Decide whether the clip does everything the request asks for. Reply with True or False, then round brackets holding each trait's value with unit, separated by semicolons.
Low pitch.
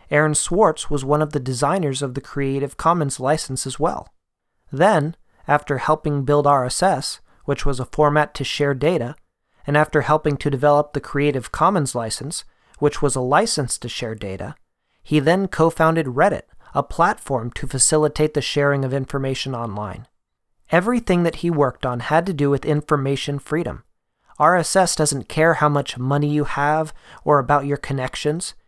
False (145 Hz)